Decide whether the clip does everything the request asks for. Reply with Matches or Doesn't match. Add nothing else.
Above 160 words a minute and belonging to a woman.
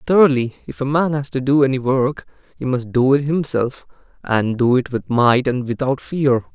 Doesn't match